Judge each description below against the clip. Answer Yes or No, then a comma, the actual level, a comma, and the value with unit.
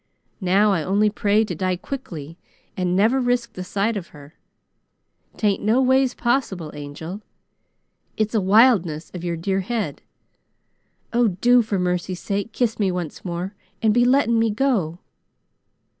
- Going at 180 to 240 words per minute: No, average, 150 wpm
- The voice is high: Yes, high, 200 Hz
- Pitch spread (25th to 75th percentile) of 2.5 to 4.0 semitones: No, average, 4.5 semitones